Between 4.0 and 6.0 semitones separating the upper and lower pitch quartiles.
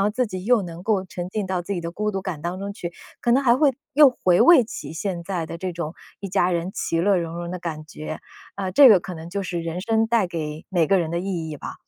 No: average, 3.2 semitones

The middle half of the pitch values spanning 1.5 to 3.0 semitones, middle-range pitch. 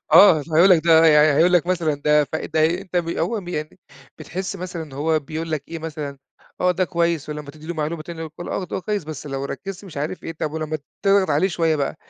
Yes: average, 2.7 semitones; medium, 160 Hz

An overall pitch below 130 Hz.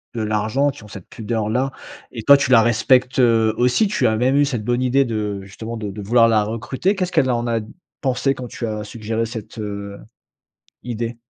Yes: low, 115 Hz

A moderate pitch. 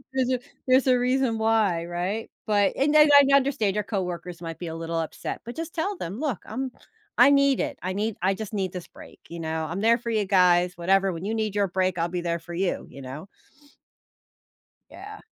No: high, 200 Hz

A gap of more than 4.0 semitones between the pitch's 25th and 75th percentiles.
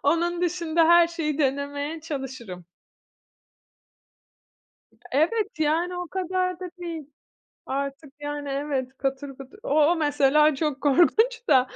No: average, 3.7 semitones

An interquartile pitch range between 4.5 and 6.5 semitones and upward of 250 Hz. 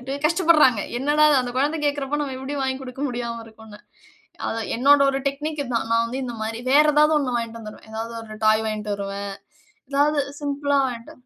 No: average, 4.1 semitones; very high, 260 Hz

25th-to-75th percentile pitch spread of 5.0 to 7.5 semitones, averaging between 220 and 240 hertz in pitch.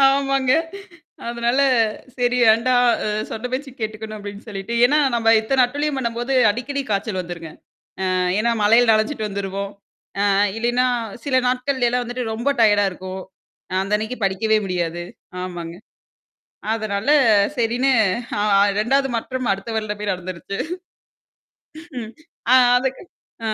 No: average, 3.8 semitones; high, 225 Hz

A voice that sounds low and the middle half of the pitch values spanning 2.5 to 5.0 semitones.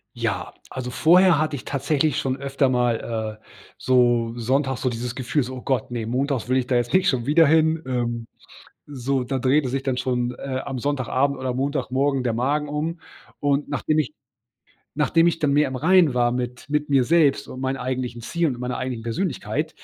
Yes: low, 130 Hz; average, 2.9 semitones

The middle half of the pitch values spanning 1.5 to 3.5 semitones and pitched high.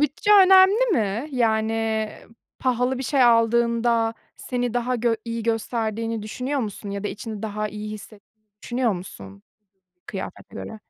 Yes: narrow, 2.5 semitones; high, 230 Hz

